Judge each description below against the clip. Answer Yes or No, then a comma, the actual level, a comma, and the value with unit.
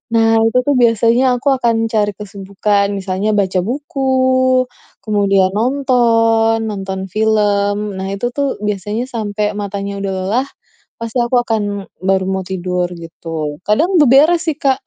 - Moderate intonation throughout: Yes, average, 3.9 semitones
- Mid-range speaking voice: No, high, 215 Hz